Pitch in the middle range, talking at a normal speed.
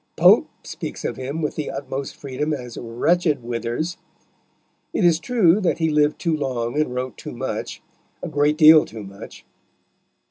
Yes: medium, 145 Hz; average, 165 wpm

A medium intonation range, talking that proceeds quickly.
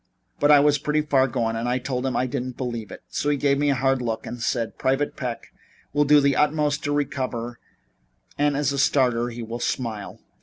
Yes: average, 3.2 semitones; fast, 220 wpm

